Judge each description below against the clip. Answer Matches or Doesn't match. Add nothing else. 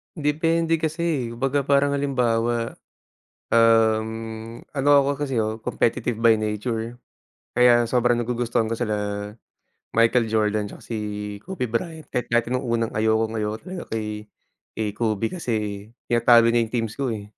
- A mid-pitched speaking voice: Doesn't match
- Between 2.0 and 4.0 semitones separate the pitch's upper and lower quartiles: Matches